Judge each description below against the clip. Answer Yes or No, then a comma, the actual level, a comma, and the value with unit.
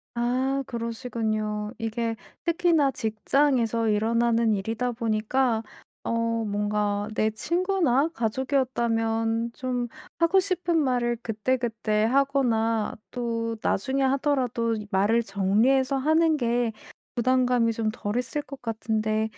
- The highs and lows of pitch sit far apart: No, average, 3.0 semitones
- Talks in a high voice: Yes, high, 235 Hz